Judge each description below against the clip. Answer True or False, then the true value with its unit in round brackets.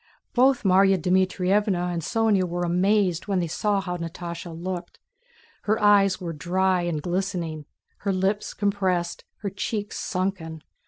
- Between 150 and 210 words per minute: False (140 wpm)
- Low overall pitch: False (185 Hz)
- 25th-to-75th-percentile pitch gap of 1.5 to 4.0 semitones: True (2.5 semitones)